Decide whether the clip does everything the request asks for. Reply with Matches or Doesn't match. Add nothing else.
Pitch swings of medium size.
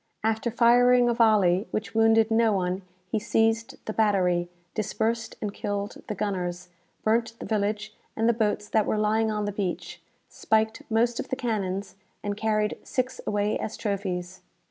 Doesn't match